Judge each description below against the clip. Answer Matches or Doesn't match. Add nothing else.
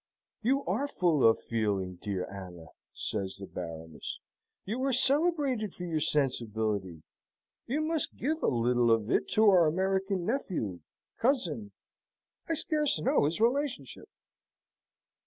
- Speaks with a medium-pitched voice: Matches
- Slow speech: Matches